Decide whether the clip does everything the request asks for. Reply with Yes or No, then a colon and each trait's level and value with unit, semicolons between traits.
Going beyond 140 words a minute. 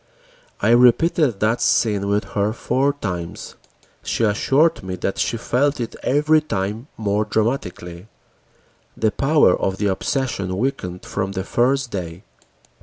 No: slow, 135 wpm